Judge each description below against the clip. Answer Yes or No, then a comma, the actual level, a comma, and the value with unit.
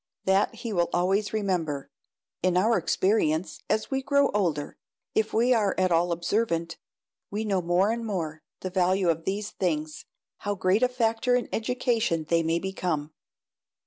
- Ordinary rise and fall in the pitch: Yes, average, 4.4 semitones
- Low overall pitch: No, high, 190 Hz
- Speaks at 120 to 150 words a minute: No, average, 160 wpm